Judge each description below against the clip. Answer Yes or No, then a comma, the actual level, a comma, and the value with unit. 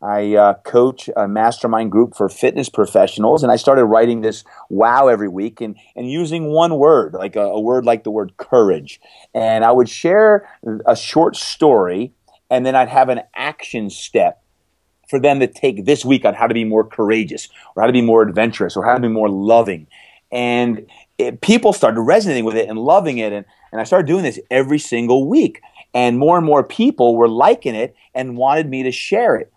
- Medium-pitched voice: No, low, 120 Hz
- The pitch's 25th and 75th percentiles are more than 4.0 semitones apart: No, average, 3.3 semitones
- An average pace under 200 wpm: No, fast, 205 wpm